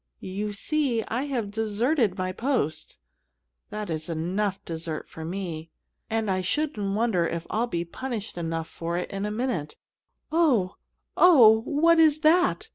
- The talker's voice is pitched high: Yes, high, 210 Hz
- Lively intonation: Yes, wide, 6.7 semitones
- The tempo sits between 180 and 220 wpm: No, average, 150 wpm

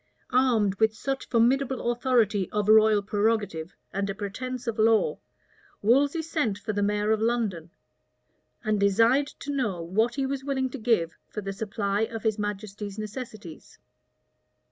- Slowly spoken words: No, average, 150 wpm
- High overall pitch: Yes, high, 220 Hz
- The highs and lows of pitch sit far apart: No, average, 3.5 semitones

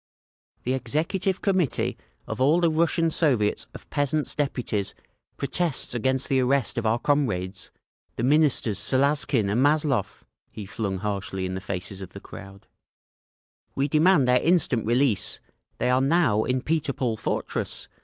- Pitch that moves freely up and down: Yes, wide, 5.9 semitones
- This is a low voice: Yes, low, 130 Hz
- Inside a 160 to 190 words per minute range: No, average, 145 wpm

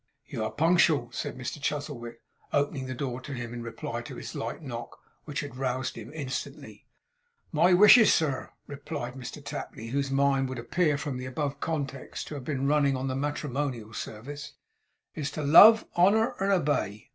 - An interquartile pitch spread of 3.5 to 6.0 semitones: No, average, 2.8 semitones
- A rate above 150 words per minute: Yes, average, 170 wpm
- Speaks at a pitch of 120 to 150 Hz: Yes, medium, 140 Hz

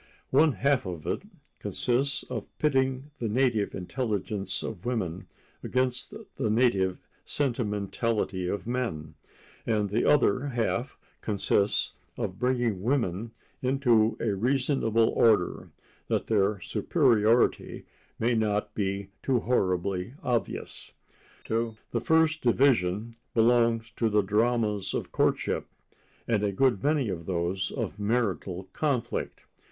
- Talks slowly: Yes, slow, 115 wpm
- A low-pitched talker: Yes, low, 115 Hz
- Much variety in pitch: No, average, 4.0 semitones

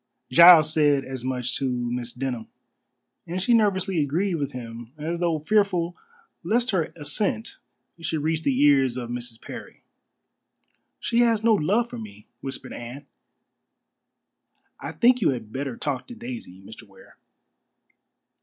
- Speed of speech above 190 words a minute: No, average, 145 wpm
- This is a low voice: No, medium, 150 Hz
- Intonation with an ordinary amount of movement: No, wide, 7.7 semitones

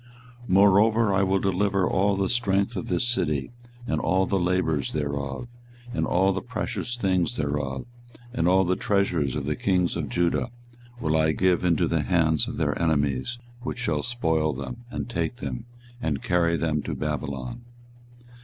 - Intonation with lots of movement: No, average, 4.6 semitones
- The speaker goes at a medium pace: Yes, average, 170 wpm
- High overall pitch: No, very low, 90 Hz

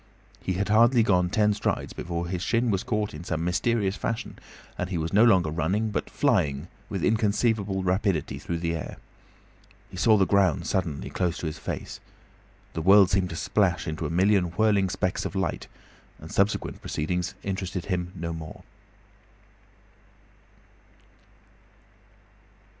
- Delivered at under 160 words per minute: Yes, average, 150 wpm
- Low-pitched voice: Yes, very low, 95 Hz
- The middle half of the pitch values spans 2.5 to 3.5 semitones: Yes, average, 3.2 semitones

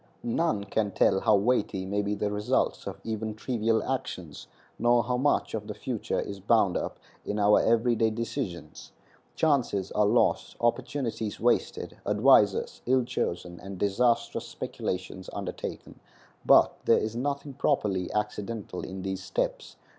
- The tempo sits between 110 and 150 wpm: Yes, average, 145 wpm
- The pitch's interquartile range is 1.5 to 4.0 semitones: Yes, average, 3.4 semitones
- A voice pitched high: No, low, 110 Hz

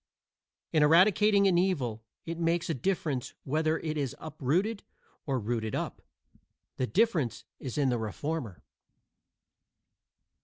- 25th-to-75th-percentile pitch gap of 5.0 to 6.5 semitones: Yes, wide, 5.6 semitones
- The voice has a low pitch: No, medium, 155 Hz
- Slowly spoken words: Yes, slow, 120 wpm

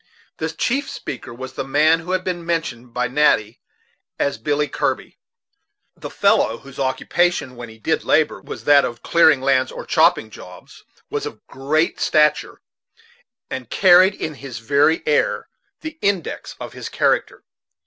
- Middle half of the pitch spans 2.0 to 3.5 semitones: No, average, 4.7 semitones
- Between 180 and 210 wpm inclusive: No, average, 155 wpm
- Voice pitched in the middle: Yes, medium, 145 Hz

